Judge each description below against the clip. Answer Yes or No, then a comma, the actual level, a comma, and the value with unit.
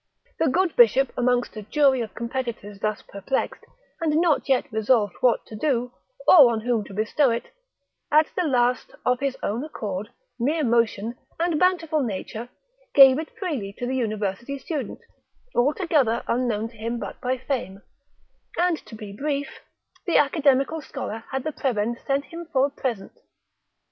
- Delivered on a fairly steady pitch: No, average, 4.6 semitones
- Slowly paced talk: No, average, 160 wpm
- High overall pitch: Yes, very high, 250 Hz